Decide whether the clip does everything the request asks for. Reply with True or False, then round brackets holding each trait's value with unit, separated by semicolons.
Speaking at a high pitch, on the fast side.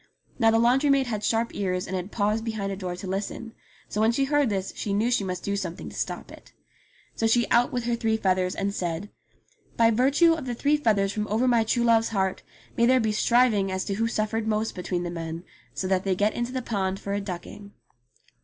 True (215 Hz; 235 wpm)